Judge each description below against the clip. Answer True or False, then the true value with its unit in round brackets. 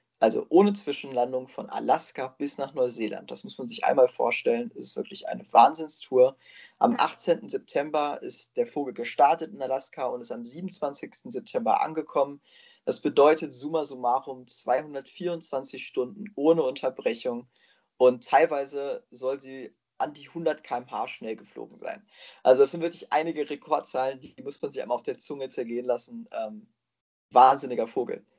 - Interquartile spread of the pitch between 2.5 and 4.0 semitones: False (4.6 semitones)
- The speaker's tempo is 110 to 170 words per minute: True (150 wpm)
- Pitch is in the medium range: True (145 Hz)